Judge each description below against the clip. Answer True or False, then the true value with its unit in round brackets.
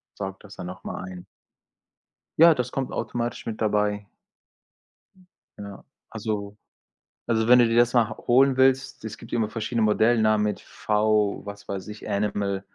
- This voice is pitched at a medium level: False (110 Hz)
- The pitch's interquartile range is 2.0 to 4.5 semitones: True (2.6 semitones)